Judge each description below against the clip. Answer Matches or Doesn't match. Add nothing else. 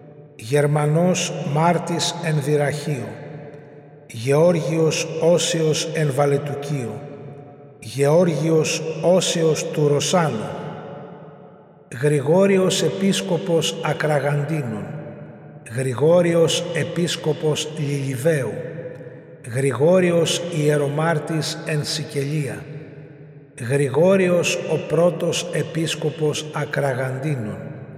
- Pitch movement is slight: Matches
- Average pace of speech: Doesn't match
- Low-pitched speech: Doesn't match